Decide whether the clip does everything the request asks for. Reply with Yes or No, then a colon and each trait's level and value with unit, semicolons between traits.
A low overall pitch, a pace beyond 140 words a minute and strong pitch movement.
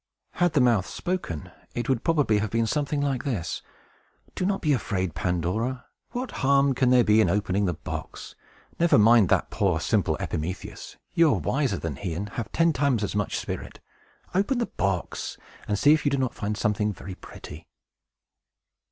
Yes: low, 115 Hz; average, 180 wpm; wide, 6.3 semitones